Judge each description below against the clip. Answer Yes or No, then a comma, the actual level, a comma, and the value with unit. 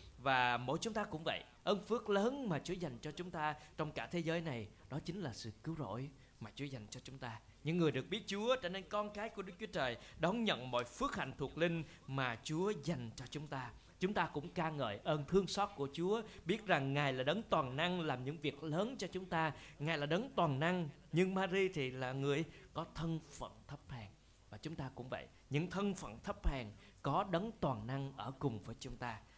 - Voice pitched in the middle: Yes, medium, 155 Hz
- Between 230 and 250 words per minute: Yes, average, 235 wpm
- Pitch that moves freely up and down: Yes, wide, 5.8 semitones